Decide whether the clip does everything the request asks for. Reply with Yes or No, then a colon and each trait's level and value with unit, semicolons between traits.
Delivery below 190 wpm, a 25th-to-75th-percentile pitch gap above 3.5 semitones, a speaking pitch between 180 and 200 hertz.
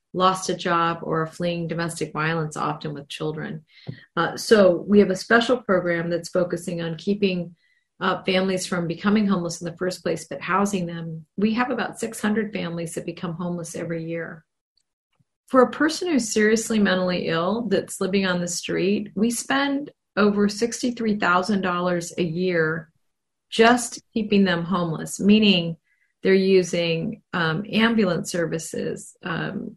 Yes: average, 145 wpm; average, 3.9 semitones; medium, 185 Hz